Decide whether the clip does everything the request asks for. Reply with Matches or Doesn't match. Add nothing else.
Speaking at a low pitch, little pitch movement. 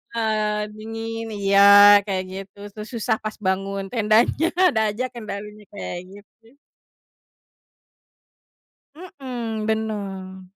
Doesn't match